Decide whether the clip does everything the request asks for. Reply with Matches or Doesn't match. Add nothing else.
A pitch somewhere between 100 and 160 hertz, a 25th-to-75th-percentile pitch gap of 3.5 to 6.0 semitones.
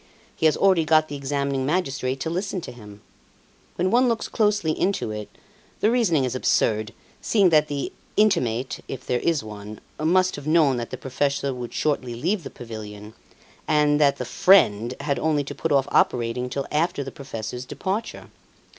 Matches